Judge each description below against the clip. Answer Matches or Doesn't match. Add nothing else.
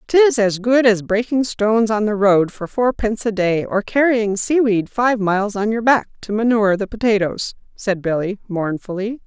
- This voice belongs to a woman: Matches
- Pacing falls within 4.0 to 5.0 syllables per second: Matches